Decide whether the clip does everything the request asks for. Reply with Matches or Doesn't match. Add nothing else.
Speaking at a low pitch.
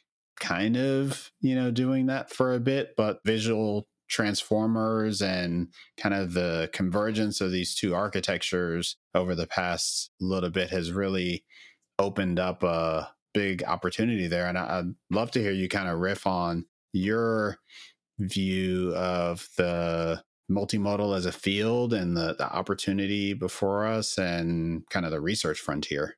Matches